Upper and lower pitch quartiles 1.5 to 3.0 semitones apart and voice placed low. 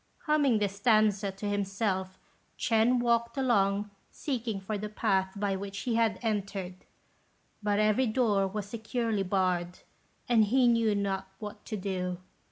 No: average, 2.7 semitones; high, 210 Hz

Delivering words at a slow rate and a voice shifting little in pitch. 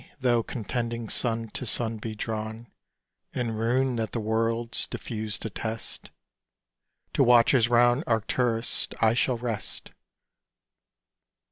Yes: slow, 110 wpm; narrow, 1.5 semitones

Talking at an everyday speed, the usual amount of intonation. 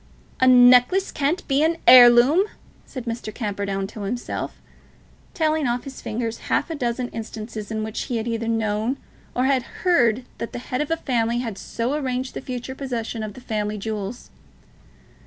Yes: average, 175 wpm; average, 3.0 semitones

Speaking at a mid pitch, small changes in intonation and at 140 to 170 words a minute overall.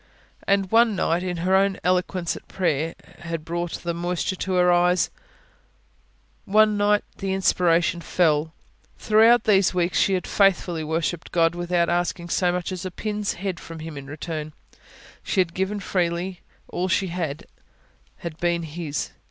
Yes: medium, 175 Hz; narrow, 2.2 semitones; average, 160 wpm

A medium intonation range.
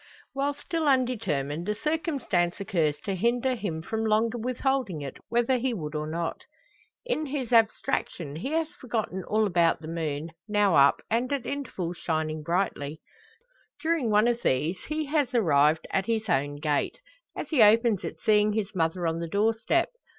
No: wide, 7.1 semitones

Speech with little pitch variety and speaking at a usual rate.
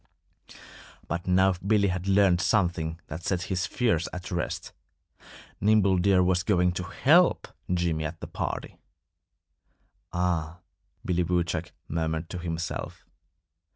No: narrow, 1.7 semitones; slow, 120 wpm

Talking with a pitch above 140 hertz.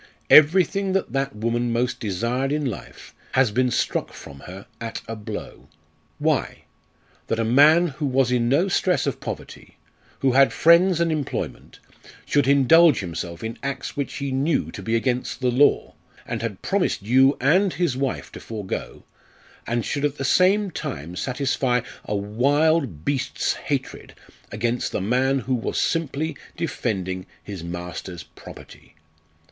No: low, 130 Hz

